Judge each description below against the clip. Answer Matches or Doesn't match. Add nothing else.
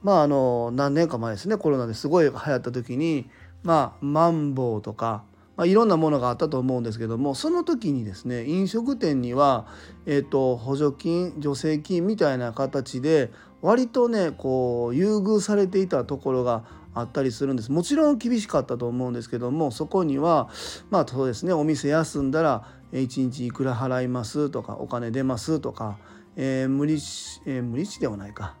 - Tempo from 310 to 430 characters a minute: Matches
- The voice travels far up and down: Doesn't match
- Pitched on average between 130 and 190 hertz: Matches